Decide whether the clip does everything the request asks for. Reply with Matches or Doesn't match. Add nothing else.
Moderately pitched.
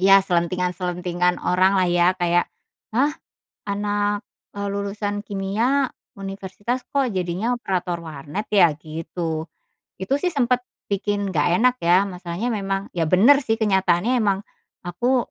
Doesn't match